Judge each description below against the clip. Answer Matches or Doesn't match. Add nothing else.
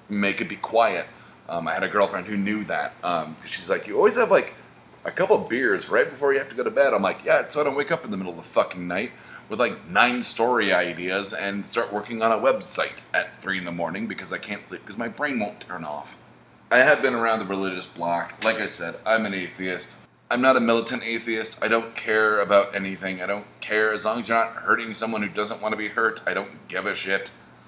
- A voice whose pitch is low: Matches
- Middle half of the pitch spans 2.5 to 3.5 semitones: Matches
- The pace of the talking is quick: Matches